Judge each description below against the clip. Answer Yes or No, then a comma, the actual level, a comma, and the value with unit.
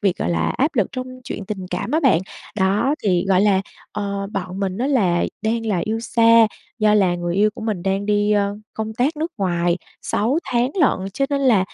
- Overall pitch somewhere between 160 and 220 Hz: Yes, high, 205 Hz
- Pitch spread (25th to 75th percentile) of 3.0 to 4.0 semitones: Yes, average, 3.7 semitones